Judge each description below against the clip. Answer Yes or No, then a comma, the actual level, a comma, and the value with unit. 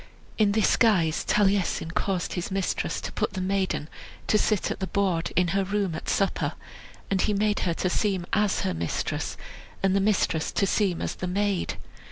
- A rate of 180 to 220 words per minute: Yes, average, 190 wpm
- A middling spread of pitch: No, narrow, 2.3 semitones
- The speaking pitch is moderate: No, high, 195 Hz